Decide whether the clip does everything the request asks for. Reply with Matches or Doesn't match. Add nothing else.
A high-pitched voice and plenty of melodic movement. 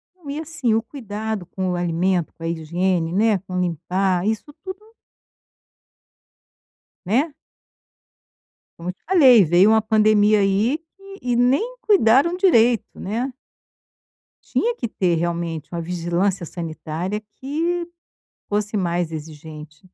Matches